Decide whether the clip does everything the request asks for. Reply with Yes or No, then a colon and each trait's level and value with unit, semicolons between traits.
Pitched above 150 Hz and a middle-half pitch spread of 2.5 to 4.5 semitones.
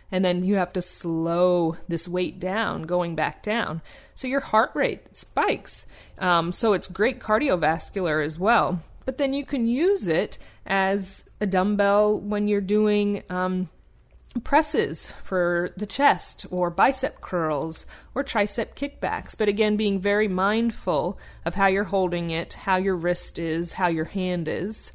Yes: high, 190 Hz; average, 3.2 semitones